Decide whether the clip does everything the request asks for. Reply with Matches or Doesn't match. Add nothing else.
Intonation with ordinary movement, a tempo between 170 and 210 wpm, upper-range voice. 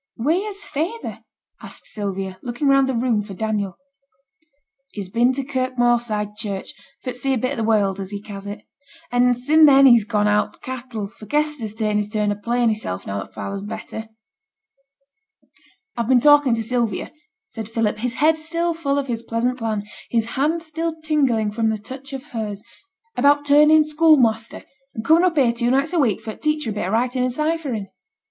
Matches